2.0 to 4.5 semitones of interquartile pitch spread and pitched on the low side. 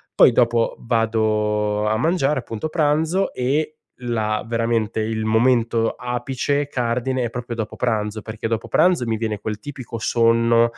Yes: narrow, 2.6 semitones; low, 115 Hz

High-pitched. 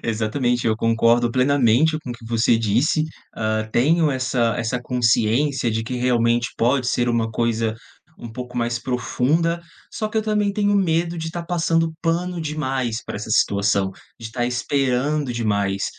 No: low, 125 Hz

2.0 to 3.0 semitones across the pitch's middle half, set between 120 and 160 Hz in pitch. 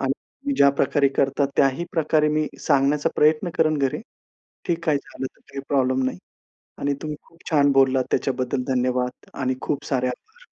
Yes: narrow, 2.6 semitones; medium, 140 Hz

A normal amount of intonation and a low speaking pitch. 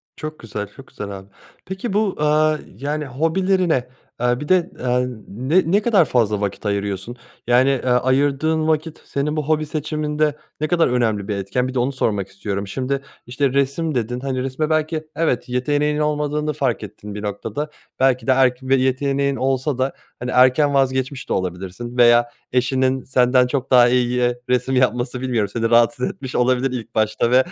Yes: average, 3.6 semitones; low, 130 Hz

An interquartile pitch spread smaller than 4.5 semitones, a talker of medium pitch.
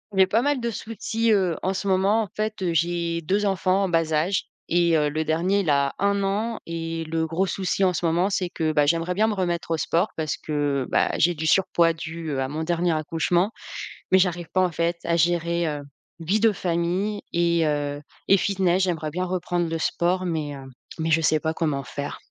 Yes: average, 2.9 semitones; medium, 170 Hz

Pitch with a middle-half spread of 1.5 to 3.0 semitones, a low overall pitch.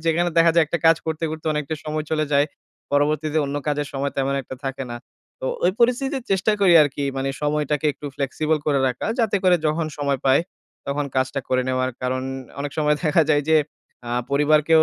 No: narrow, 2.4 semitones; medium, 150 Hz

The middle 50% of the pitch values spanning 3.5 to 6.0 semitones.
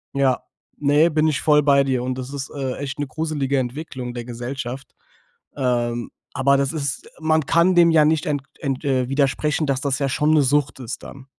No: narrow, 2.4 semitones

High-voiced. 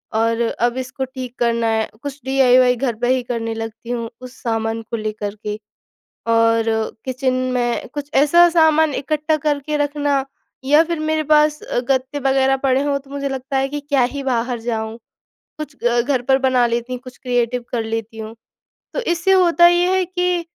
Yes: very high, 260 Hz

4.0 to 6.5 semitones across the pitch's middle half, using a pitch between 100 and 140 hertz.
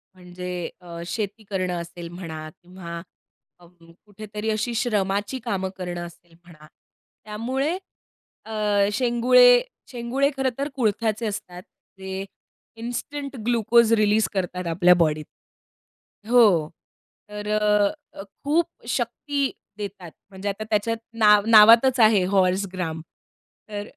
No: average, 4.5 semitones; high, 210 Hz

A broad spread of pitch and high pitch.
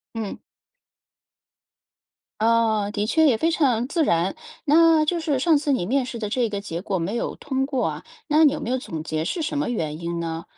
Yes: wide, 7.1 semitones; high, 240 Hz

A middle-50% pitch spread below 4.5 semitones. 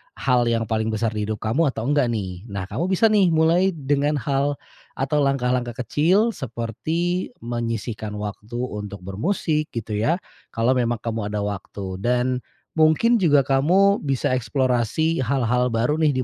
No: average, 5.3 semitones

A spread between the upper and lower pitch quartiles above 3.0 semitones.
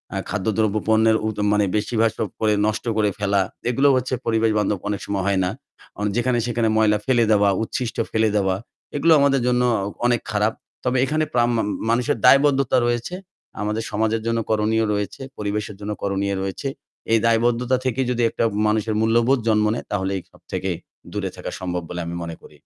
No: narrow, 2.5 semitones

